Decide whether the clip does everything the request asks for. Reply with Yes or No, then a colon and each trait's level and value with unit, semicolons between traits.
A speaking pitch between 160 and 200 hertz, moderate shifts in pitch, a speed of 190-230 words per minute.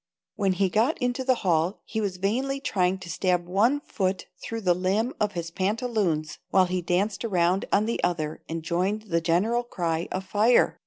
Yes: high, 190 Hz; average, 3.9 semitones; average, 195 wpm